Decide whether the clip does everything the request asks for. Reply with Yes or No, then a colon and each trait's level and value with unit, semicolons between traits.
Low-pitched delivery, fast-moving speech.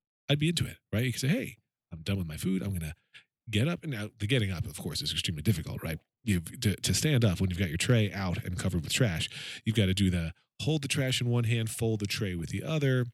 Yes: low, 110 Hz; fast, 285 wpm